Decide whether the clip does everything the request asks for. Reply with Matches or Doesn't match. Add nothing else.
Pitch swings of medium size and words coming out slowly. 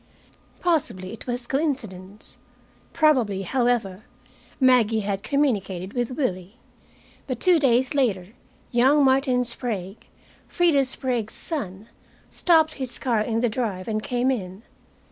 Matches